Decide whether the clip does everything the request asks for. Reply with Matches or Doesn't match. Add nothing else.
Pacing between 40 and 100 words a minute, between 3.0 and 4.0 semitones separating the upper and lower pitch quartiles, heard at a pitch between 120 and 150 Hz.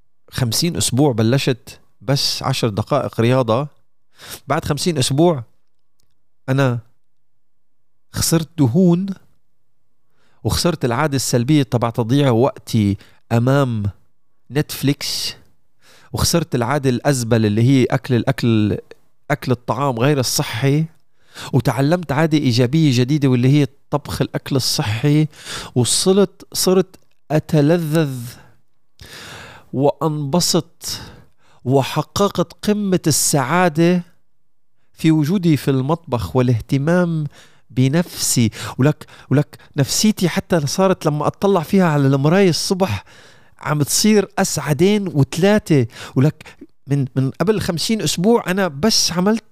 Doesn't match